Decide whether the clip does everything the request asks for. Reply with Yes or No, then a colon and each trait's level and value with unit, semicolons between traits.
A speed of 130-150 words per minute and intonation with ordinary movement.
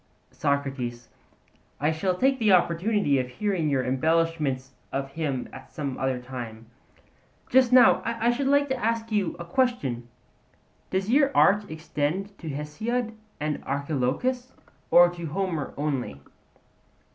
No: slow, 135 wpm; wide, 8.2 semitones